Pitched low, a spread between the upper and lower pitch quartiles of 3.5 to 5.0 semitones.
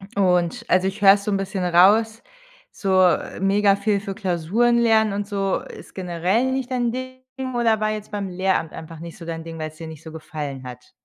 No: high, 195 Hz; average, 4.2 semitones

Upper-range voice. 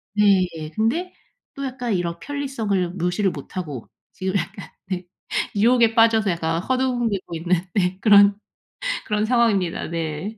Yes: high, 200 Hz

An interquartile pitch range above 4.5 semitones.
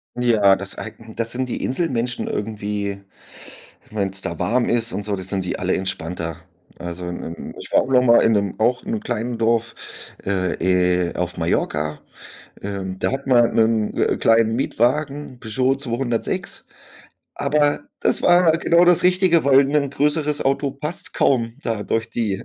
Yes: wide, 5.6 semitones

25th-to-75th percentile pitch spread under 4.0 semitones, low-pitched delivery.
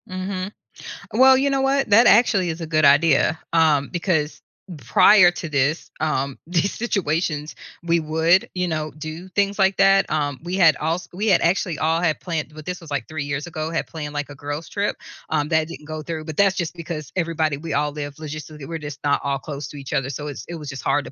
No: average, 3.4 semitones; medium, 160 Hz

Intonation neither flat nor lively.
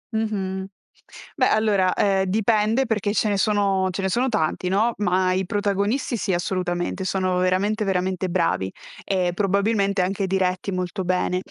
No: narrow, 2.1 semitones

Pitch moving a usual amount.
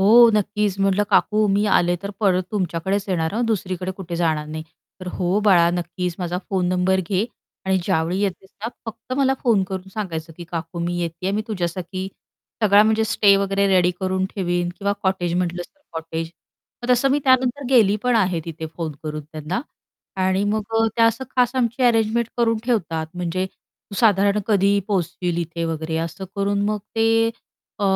Yes: average, 3.4 semitones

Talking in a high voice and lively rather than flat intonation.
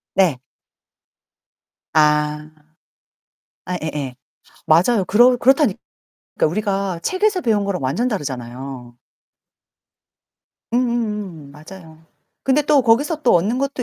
Yes: high, 195 Hz; wide, 8.2 semitones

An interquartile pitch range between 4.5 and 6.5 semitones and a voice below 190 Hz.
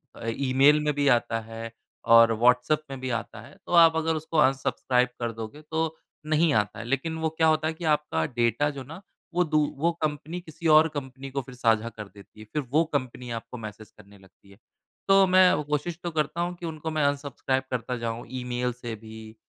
Yes: average, 5.2 semitones; low, 135 Hz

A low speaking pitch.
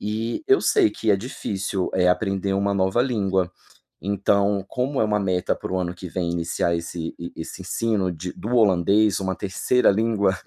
Yes: low, 100 Hz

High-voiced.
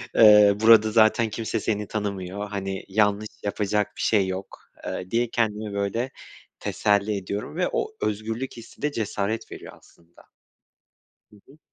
No: low, 105 Hz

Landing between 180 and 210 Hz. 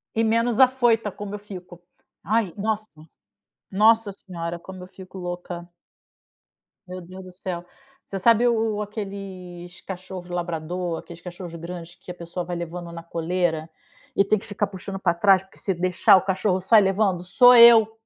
Yes: medium, 185 Hz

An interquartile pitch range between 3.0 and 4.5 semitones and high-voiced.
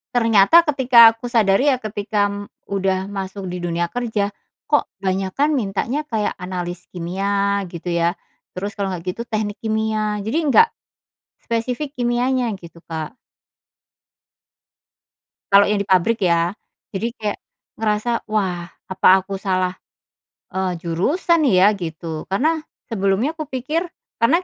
Yes: average, 4.0 semitones; high, 205 Hz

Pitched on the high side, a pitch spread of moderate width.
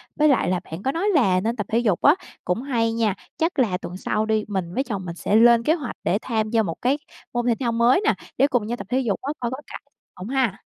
Yes: high, 230 Hz; average, 4.3 semitones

